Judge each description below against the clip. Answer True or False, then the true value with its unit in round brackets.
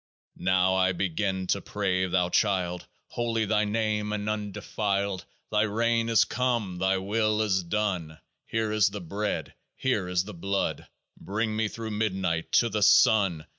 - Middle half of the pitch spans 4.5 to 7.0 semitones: False (2.5 semitones)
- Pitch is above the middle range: False (105 Hz)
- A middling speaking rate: True (155 wpm)